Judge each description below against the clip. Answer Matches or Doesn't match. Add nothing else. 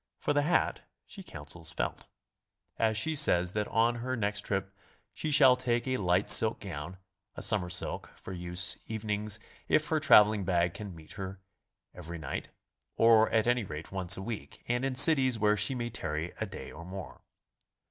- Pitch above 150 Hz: Doesn't match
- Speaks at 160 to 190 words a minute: Matches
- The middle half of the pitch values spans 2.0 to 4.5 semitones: Doesn't match